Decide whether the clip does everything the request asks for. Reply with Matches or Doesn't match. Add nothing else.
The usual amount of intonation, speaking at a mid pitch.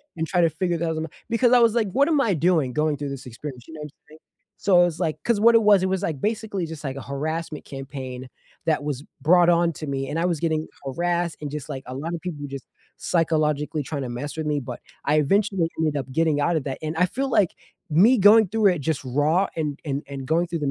Matches